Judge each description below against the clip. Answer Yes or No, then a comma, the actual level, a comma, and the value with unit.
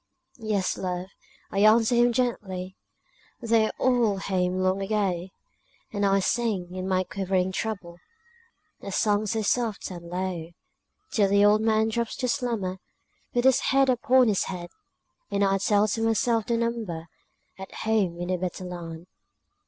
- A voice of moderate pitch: No, high, 200 Hz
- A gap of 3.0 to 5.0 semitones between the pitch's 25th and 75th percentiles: Yes, average, 3.4 semitones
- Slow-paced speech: No, average, 155 wpm